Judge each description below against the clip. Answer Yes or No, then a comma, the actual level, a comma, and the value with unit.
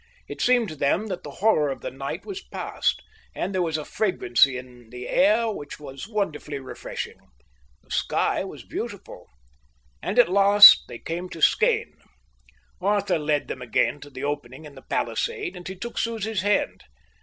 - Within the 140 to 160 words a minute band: No, average, 175 wpm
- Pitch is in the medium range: Yes, medium, 165 Hz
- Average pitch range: No, wide, 6.9 semitones